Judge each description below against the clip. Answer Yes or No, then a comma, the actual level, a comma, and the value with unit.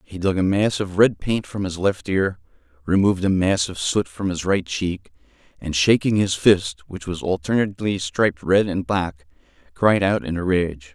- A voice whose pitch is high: No, very low, 90 Hz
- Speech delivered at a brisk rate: No, average, 195 wpm